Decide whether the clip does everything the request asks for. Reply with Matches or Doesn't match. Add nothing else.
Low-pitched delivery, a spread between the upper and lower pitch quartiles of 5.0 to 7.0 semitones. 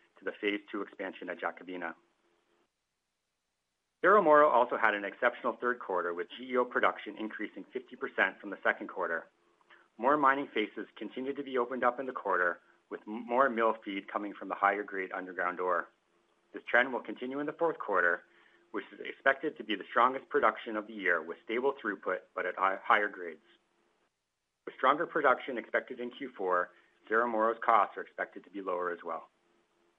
Matches